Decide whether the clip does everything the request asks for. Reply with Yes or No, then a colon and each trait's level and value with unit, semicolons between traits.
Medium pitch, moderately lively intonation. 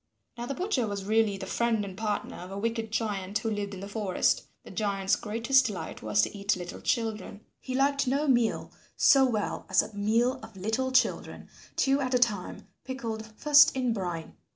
No: high, 220 Hz; average, 3.9 semitones